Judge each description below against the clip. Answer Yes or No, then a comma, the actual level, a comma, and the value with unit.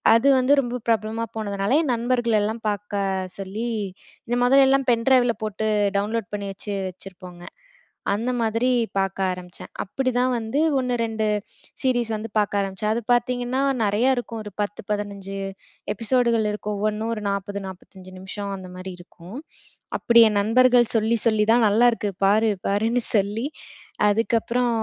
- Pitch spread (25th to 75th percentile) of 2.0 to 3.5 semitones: Yes, average, 3.0 semitones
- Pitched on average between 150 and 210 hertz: No, high, 220 Hz